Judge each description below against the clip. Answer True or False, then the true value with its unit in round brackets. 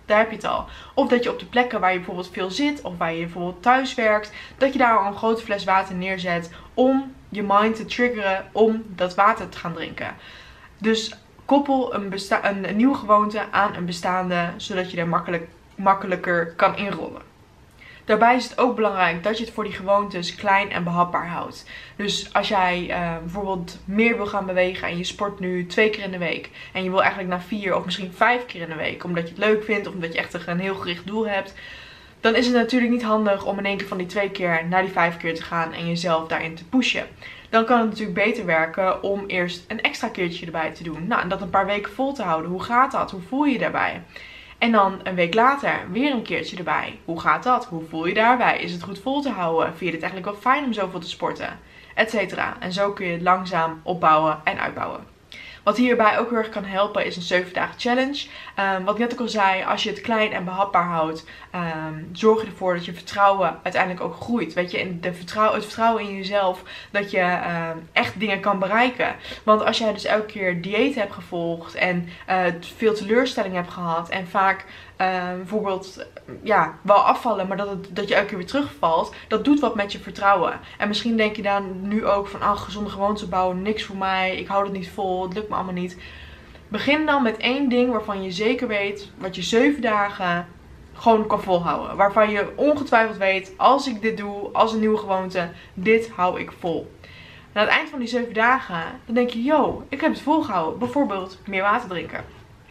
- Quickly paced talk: True (225 wpm)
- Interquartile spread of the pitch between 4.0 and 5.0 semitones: False (3.6 semitones)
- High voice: True (200 Hz)